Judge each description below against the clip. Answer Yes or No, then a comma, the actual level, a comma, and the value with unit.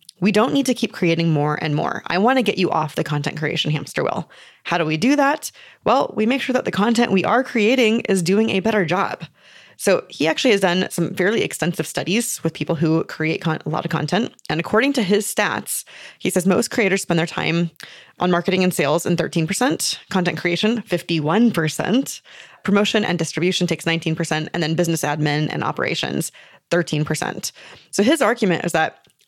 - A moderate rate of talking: Yes, average, 195 wpm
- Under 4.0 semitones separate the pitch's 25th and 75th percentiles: No, average, 4.6 semitones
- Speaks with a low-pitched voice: No, medium, 180 Hz